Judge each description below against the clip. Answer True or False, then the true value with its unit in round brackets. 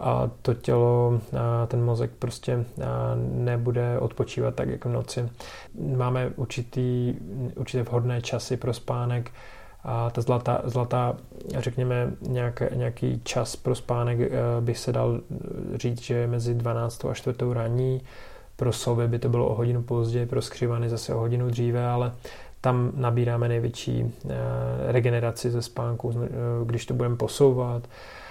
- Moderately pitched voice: False (120 Hz)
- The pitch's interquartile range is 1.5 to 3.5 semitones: False (0.9 semitones)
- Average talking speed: True (135 wpm)